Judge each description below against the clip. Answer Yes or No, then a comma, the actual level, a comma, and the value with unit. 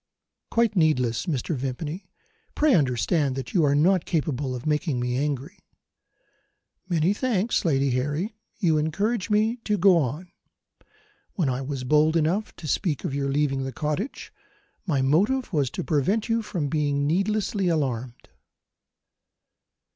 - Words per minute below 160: Yes, average, 140 wpm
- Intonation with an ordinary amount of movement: No, wide, 5.8 semitones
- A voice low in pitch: No, medium, 155 Hz